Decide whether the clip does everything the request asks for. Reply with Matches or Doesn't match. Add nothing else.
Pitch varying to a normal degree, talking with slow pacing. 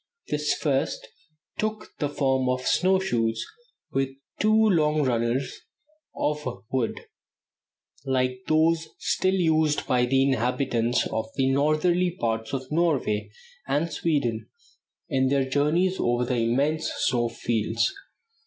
Matches